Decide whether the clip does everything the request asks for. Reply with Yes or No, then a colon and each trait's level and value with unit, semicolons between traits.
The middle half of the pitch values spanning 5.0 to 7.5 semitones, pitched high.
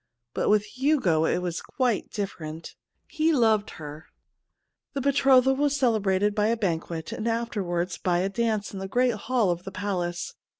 Yes: wide, 5.6 semitones; high, 210 Hz